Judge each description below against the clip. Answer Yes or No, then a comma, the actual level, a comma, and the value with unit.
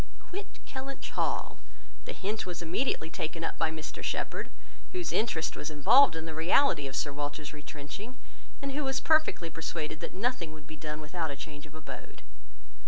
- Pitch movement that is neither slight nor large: No, wide, 7.3 semitones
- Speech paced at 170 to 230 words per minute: Yes, average, 175 wpm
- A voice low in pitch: No, medium, 160 Hz